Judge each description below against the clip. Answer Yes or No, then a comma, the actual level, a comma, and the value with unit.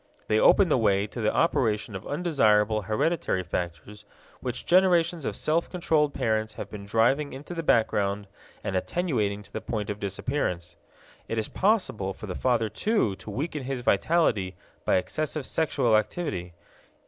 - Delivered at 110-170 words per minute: Yes, average, 160 wpm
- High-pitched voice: No, low, 110 Hz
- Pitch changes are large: Yes, wide, 6.9 semitones